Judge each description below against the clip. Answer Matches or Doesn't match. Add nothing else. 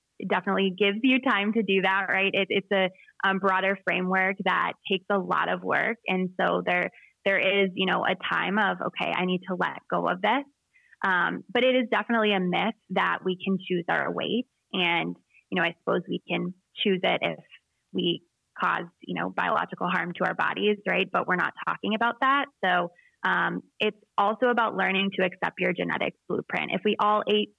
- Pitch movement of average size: Doesn't match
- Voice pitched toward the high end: Matches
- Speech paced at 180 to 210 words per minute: Matches